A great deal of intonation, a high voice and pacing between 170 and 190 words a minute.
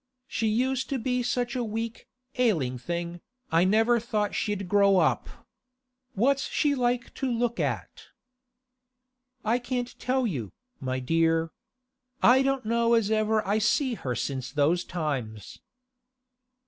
No: wide, 6.3 semitones; high, 220 Hz; slow, 135 wpm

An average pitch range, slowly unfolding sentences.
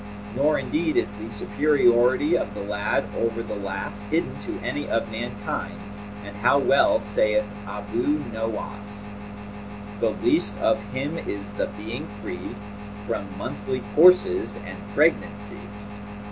No: narrow, 2.3 semitones; slow, 130 wpm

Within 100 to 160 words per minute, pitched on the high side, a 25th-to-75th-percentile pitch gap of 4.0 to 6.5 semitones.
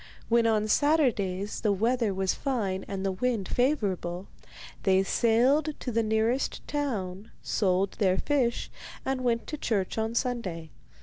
Yes: average, 140 wpm; high, 220 Hz; average, 4.6 semitones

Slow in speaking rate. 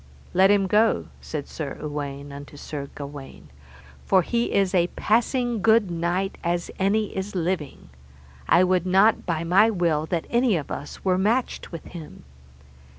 No: average, 155 wpm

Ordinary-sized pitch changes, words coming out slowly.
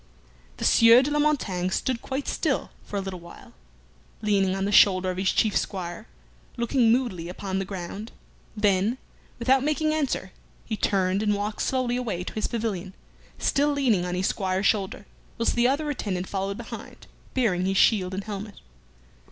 No: average, 4.3 semitones; average, 170 wpm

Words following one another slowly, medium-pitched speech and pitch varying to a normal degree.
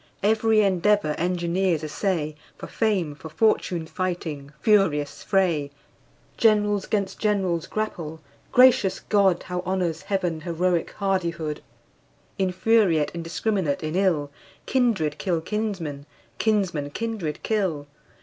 Yes: slow, 105 wpm; medium, 180 Hz; average, 4.4 semitones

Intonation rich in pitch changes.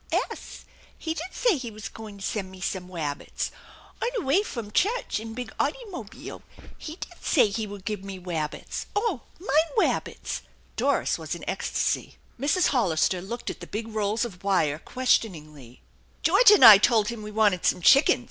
Yes: wide, 6.9 semitones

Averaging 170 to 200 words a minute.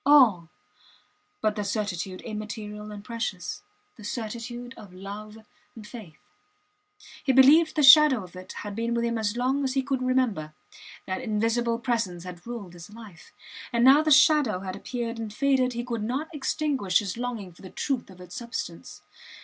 Yes: average, 175 wpm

